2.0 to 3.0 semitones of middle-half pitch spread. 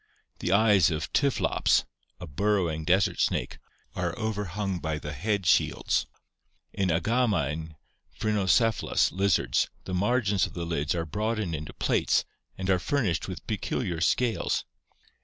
No: average, 4.5 semitones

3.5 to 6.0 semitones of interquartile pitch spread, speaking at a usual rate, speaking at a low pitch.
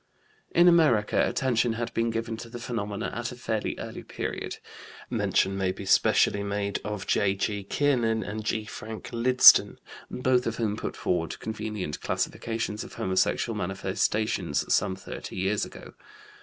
No: narrow, 2.6 semitones; average, 145 wpm; low, 110 Hz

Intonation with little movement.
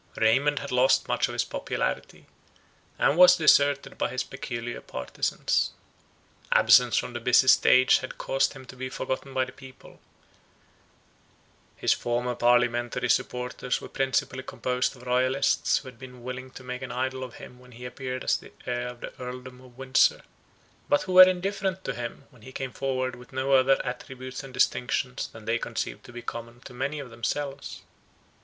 Yes: narrow, 1.4 semitones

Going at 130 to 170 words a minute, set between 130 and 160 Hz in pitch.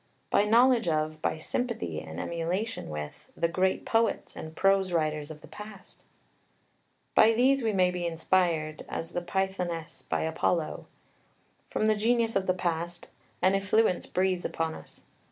No: average, 155 wpm; medium, 180 Hz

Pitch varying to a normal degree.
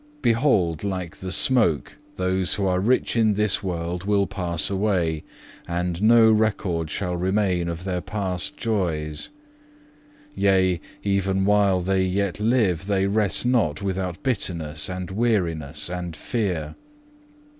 Yes: average, 3.0 semitones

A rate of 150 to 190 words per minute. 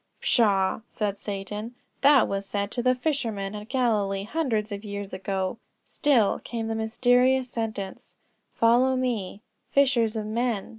No: average, 140 wpm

